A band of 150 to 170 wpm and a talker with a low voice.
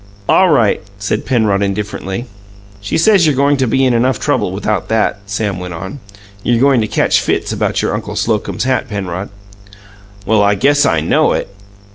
No: average, 180 wpm; low, 110 Hz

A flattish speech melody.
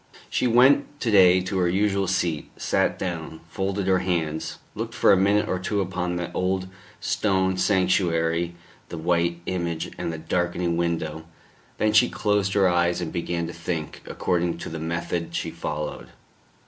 Yes: narrow, 2.2 semitones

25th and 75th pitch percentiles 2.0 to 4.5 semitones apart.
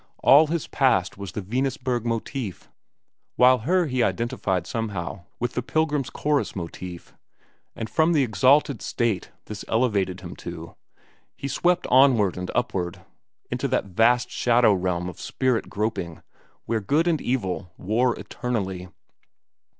No: wide, 5.6 semitones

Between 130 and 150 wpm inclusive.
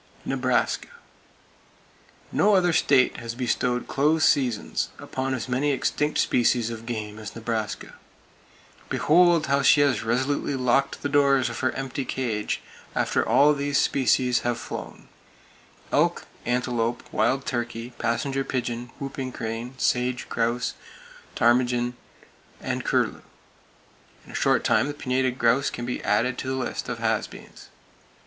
Yes: average, 140 wpm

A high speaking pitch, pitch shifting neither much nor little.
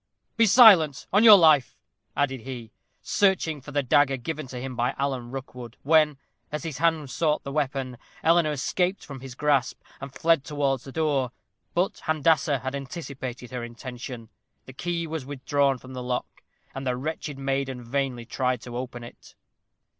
No: low, 135 Hz; average, 3.4 semitones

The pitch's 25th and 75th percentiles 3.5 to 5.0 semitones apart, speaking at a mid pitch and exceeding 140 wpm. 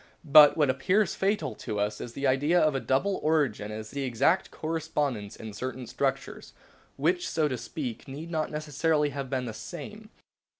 Yes: average, 4.0 semitones; medium, 145 Hz; average, 175 wpm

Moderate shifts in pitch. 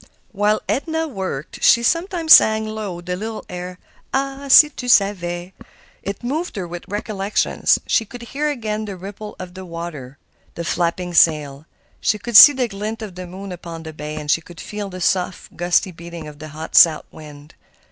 Yes: average, 4.3 semitones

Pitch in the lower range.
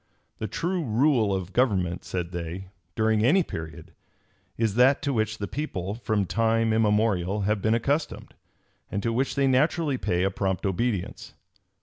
Yes: low, 110 Hz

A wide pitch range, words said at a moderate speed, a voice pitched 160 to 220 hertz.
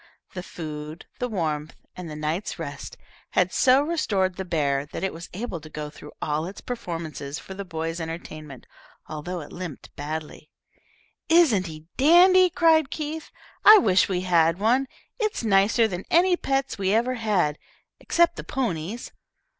Yes: wide, 8.2 semitones; average, 160 wpm; medium, 185 Hz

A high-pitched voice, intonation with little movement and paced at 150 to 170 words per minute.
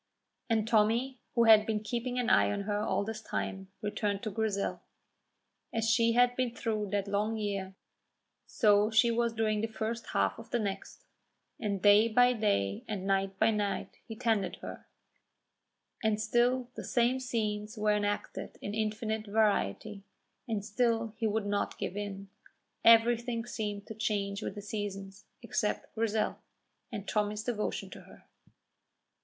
Yes: high, 215 Hz; narrow, 1.9 semitones; average, 155 wpm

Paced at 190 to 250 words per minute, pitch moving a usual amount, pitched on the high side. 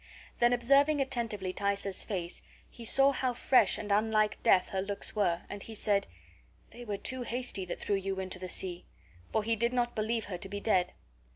Yes: average, 195 wpm; average, 3.7 semitones; high, 210 Hz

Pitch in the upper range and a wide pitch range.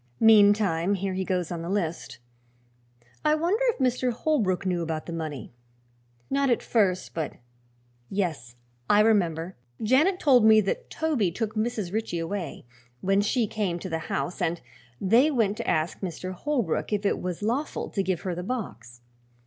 No: high, 200 Hz; average, 5.0 semitones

